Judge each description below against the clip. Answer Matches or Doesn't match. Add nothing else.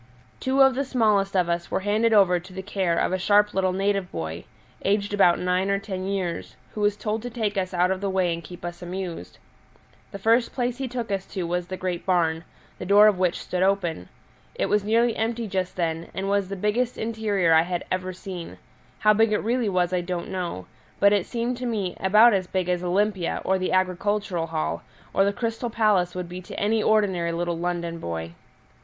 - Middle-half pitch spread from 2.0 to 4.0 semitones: Matches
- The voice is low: Doesn't match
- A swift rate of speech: Matches